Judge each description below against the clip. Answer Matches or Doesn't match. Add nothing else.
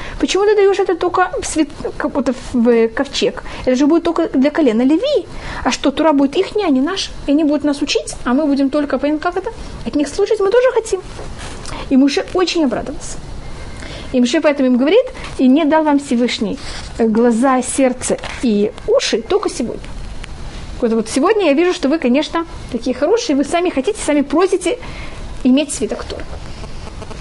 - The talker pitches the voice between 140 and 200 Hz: Doesn't match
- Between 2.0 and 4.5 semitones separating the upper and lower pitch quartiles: Doesn't match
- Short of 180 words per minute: Doesn't match